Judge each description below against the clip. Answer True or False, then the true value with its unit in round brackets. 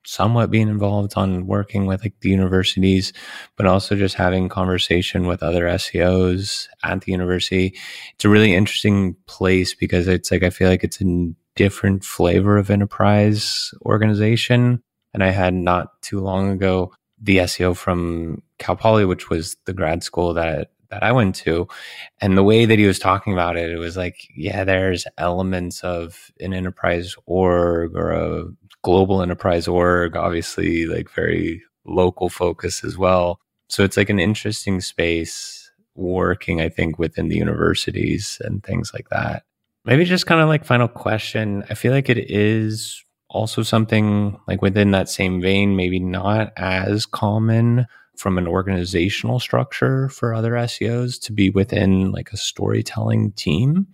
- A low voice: True (95 Hz)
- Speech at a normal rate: True (160 wpm)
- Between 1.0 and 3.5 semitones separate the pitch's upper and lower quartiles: True (2.8 semitones)